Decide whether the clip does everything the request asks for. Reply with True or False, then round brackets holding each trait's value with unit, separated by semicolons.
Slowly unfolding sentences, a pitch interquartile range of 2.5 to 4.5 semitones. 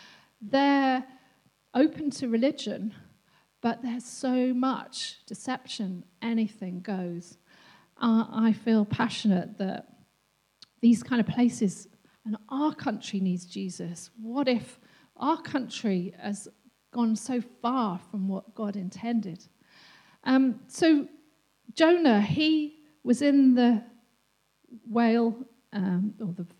True (110 wpm; 4.0 semitones)